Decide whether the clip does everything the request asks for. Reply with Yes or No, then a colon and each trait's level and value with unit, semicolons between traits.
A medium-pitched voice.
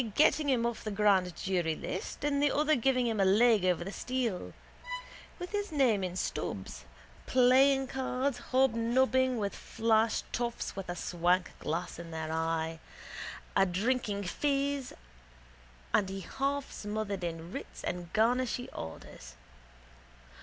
No: high, 220 Hz